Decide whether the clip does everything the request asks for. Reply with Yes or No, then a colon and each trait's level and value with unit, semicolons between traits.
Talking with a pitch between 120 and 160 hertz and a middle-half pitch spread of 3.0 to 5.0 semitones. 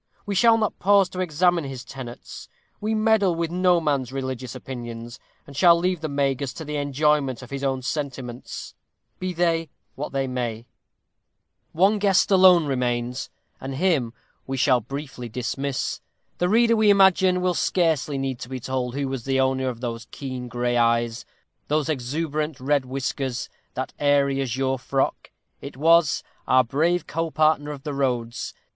Yes: medium, 140 Hz; average, 4.6 semitones